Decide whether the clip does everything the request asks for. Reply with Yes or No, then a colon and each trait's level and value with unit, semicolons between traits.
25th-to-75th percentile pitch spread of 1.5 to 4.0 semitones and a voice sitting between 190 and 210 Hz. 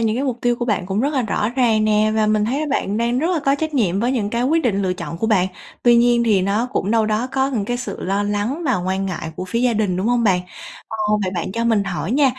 No: average, 3.5 semitones; high, 220 Hz